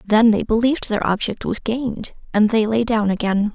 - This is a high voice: Yes, high, 220 Hz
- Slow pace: No, fast, 205 wpm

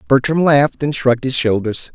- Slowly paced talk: No, average, 185 wpm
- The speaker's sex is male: Yes, male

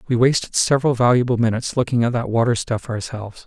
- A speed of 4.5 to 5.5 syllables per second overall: No, 6.7 syllables/s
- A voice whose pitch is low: Yes, low, 120 Hz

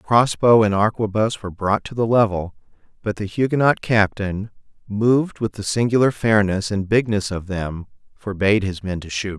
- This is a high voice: No, low, 105 Hz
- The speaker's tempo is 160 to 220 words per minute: Yes, average, 175 wpm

